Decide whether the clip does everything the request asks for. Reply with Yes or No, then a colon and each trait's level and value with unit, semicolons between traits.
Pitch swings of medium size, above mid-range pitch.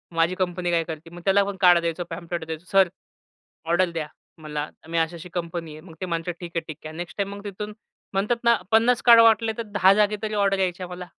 No: average, 3.2 semitones; medium, 180 Hz